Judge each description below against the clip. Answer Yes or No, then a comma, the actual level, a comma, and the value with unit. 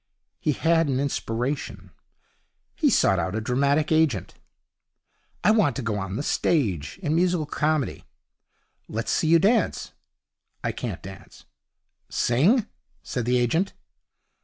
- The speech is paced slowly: Yes, slow, 130 wpm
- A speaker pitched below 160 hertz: Yes, medium, 140 Hz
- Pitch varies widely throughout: Yes, wide, 6.4 semitones